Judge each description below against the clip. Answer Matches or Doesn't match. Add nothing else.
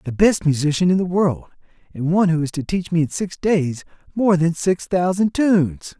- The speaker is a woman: Doesn't match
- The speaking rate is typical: Doesn't match